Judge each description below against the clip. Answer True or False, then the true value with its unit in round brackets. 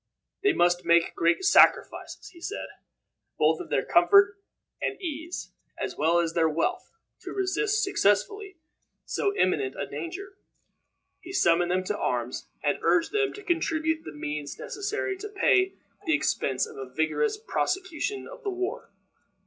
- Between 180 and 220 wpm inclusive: False (155 wpm)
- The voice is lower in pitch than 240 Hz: False (330 Hz)